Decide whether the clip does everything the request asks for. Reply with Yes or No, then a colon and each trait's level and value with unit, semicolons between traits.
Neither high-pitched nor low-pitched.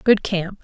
No: high, 195 Hz